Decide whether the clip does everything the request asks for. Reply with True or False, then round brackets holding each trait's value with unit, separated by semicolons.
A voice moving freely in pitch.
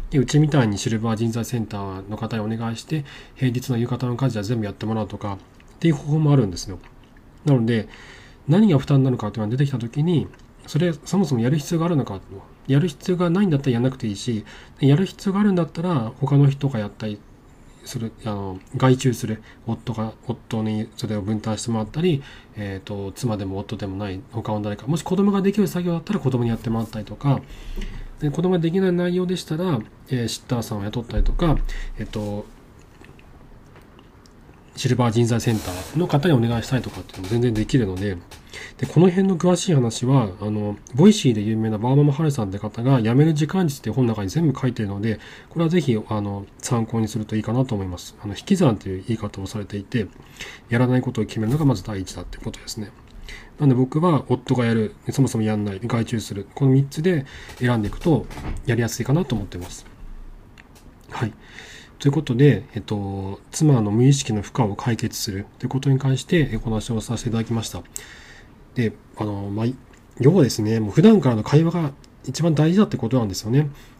False (4.7 semitones)